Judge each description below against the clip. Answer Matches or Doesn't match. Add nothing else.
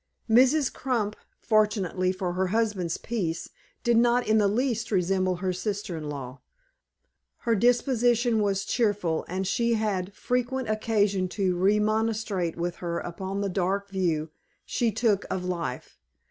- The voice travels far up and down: Doesn't match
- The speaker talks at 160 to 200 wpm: Doesn't match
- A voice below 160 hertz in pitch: Doesn't match